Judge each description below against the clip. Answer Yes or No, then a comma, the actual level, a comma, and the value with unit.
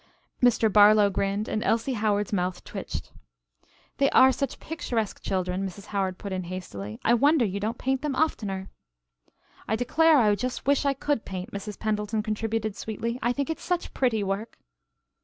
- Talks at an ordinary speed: Yes, average, 170 wpm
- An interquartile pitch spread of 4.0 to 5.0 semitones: Yes, average, 4.3 semitones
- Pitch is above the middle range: Yes, high, 215 Hz